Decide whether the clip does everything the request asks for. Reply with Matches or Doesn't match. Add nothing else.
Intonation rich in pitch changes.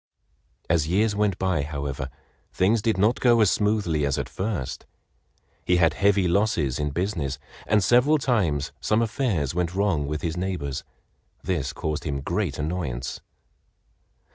Matches